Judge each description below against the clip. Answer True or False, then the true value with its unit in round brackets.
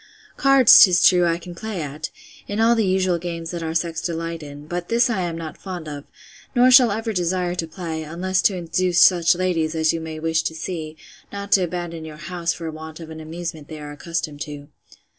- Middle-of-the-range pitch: True (170 Hz)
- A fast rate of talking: True (215 wpm)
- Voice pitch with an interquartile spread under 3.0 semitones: True (2.5 semitones)